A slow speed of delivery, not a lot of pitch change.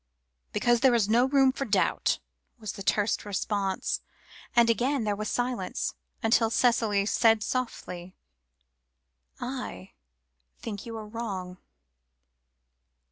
No: slow, 115 wpm; average, 3.2 semitones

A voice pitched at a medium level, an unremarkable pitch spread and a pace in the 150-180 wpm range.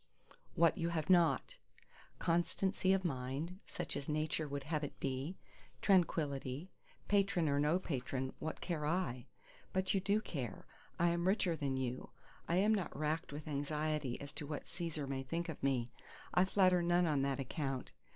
Yes: medium, 155 Hz; average, 4.2 semitones; average, 170 wpm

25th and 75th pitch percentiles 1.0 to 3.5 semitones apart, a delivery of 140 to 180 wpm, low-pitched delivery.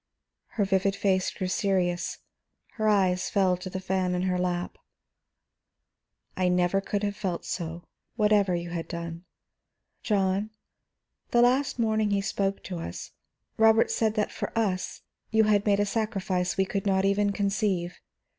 No: narrow, 2.5 semitones; average, 155 wpm; high, 195 Hz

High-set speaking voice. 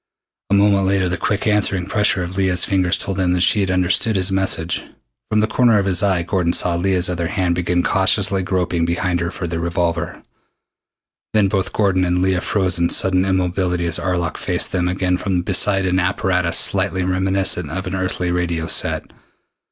No: very low, 90 Hz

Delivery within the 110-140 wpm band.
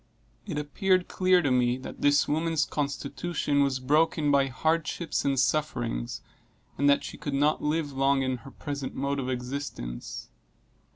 No: average, 155 wpm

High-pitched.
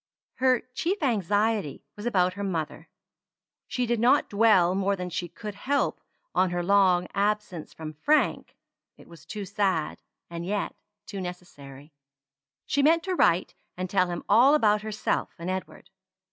Yes: high, 200 Hz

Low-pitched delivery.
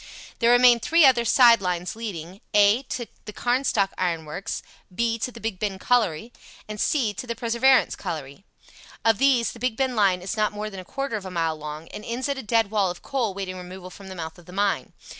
No: high, 210 Hz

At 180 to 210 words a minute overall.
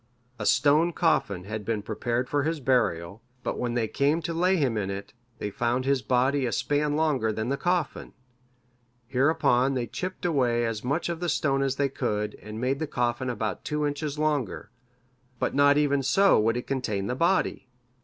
Yes: average, 190 wpm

